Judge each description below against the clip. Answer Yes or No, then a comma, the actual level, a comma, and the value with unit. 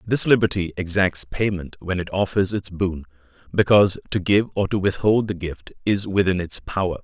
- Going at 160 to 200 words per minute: Yes, average, 180 wpm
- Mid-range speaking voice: No, very low, 95 Hz